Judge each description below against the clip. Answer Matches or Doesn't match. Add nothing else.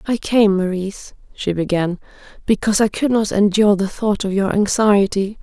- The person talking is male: Doesn't match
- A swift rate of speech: Doesn't match